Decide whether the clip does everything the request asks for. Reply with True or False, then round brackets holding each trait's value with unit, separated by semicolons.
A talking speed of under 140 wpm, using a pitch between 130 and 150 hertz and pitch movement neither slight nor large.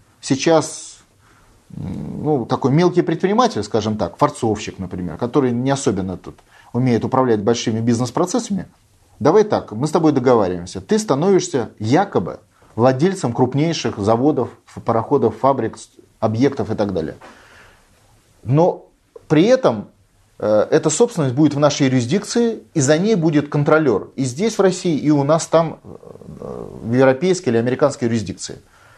False (130 wpm; 135 Hz; 6.3 semitones)